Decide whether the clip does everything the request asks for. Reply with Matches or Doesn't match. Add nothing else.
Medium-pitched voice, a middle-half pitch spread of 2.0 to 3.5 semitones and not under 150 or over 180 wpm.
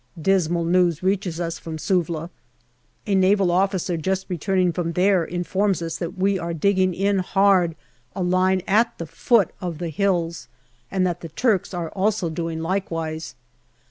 Matches